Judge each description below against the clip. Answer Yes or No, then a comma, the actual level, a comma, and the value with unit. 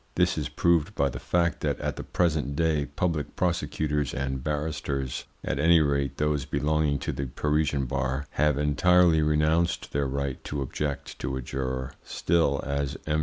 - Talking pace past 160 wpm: Yes, average, 170 wpm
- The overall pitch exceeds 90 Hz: No, very low, 75 Hz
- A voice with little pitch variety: Yes, narrow, 2.1 semitones